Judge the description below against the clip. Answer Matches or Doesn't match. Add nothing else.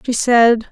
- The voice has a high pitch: Matches